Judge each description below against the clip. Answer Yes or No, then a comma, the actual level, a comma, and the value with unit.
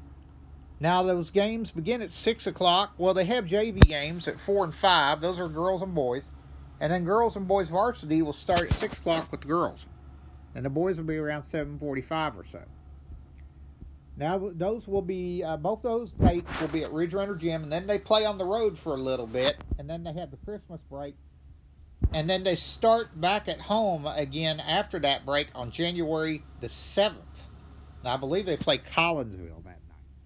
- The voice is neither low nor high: Yes, medium, 160 Hz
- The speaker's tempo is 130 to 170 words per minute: No, average, 190 wpm